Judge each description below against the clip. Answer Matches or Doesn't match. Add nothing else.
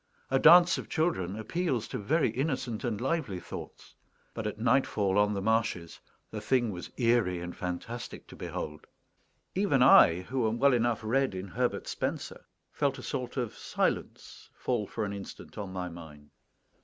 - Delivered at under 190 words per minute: Matches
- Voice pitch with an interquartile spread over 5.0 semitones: Matches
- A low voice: Matches